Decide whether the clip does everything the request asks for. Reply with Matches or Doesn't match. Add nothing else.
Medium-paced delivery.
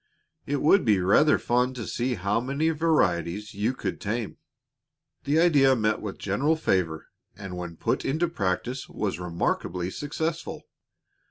Matches